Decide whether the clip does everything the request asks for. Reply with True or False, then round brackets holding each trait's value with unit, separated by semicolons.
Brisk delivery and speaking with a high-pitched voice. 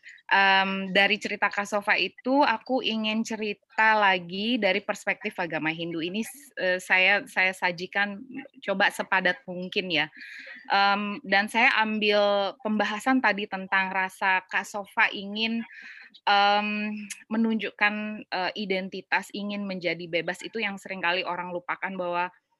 False (125 wpm; 200 Hz)